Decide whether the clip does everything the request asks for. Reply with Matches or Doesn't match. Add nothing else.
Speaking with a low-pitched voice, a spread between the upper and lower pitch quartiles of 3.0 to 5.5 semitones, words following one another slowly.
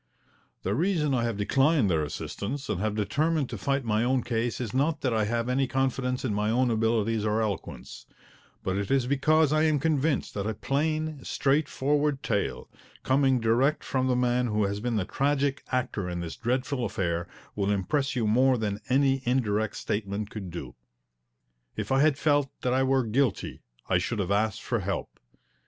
Doesn't match